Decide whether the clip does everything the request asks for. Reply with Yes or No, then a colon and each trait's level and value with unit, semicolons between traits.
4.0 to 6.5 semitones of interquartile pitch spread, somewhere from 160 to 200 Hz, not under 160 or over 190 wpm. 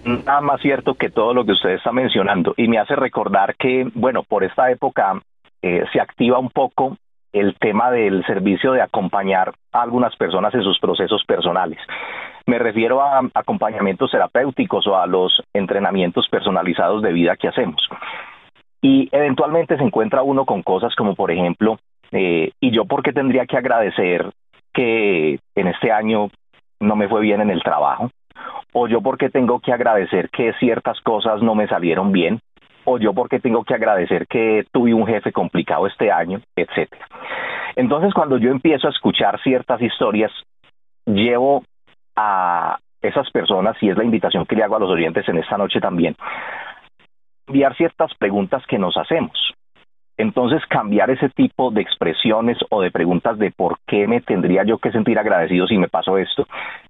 No: average, 4.7 semitones; low, 120 Hz; average, 170 wpm